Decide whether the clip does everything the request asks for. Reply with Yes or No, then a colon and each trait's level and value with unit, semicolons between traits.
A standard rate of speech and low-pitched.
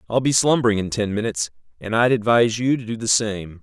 No: fast, 230 wpm; low, 110 Hz